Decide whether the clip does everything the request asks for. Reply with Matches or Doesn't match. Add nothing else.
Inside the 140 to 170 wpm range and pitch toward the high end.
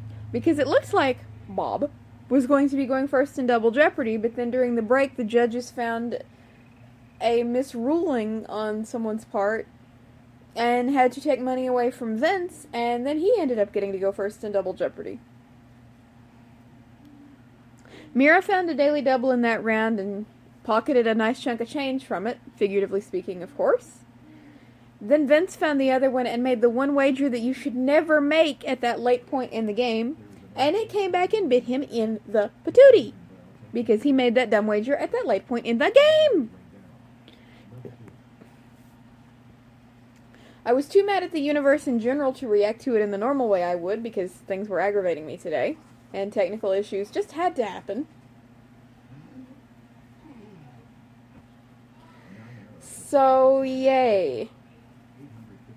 Matches